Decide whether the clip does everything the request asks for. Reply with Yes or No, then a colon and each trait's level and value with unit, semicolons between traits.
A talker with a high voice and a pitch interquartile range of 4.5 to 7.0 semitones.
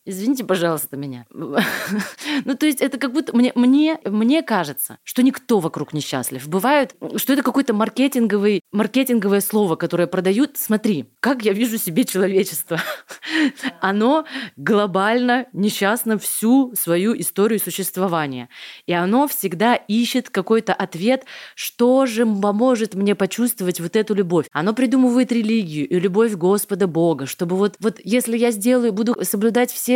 Yes: high, 215 Hz; average, 4.9 semitones